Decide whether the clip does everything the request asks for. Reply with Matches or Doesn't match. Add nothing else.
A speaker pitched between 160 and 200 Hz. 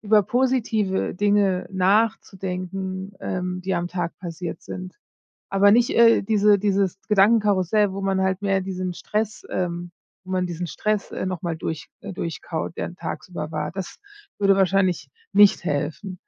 Matches